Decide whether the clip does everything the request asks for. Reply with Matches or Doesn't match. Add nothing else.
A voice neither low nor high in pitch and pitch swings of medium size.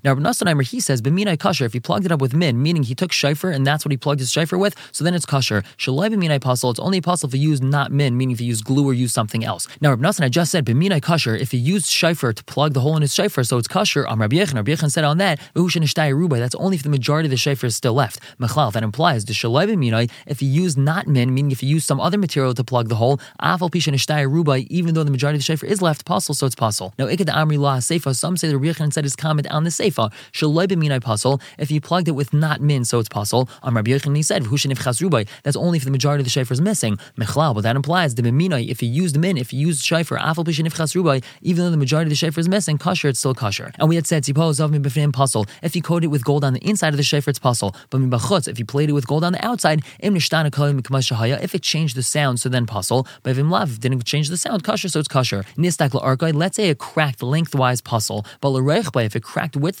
Matches